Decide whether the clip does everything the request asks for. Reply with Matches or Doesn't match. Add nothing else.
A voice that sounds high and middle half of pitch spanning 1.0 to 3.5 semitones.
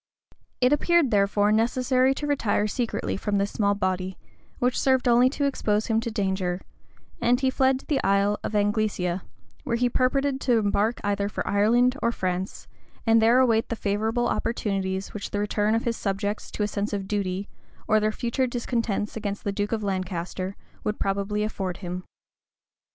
Matches